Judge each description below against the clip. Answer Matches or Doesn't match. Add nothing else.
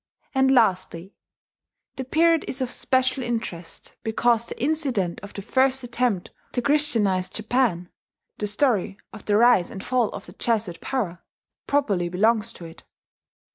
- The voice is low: Doesn't match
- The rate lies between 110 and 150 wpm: Matches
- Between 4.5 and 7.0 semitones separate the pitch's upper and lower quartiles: Matches